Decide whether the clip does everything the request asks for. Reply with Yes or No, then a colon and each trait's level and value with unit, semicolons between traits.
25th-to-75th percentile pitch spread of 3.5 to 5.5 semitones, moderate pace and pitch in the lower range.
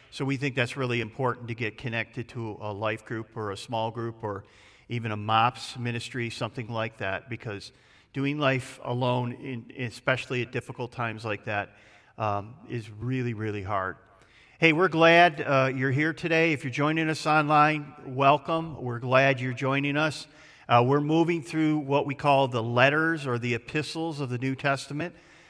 Yes: average, 4.0 semitones; average, 175 wpm; low, 130 Hz